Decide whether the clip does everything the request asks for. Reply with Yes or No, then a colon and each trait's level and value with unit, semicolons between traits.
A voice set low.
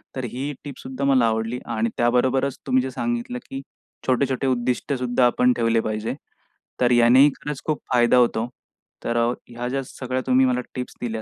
Yes: low, 125 Hz